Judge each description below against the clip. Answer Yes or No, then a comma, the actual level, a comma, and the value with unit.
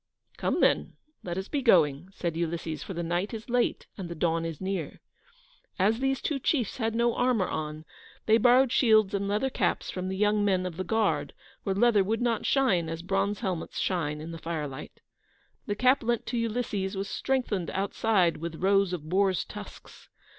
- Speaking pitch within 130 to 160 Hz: No, high, 195 Hz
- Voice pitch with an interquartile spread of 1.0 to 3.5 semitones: No, average, 4.8 semitones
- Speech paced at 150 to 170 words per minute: No, average, 190 wpm